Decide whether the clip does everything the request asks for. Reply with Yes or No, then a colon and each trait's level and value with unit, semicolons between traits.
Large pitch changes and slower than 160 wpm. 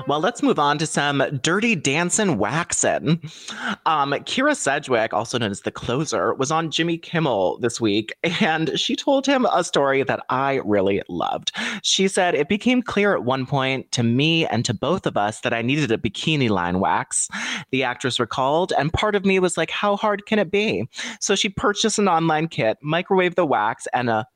No: wide, 7.7 semitones; average, 195 wpm